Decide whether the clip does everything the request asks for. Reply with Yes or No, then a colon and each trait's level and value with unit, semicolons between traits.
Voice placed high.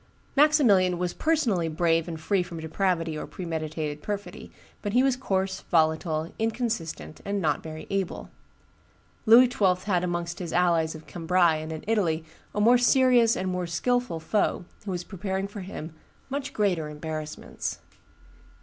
No: medium, 180 Hz